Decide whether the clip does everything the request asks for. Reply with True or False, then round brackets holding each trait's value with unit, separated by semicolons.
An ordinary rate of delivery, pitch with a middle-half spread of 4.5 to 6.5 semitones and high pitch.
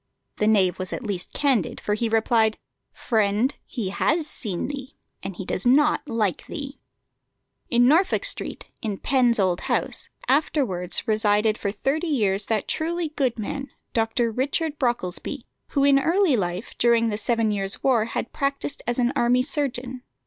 True (160 wpm; 4.8 semitones; 240 Hz)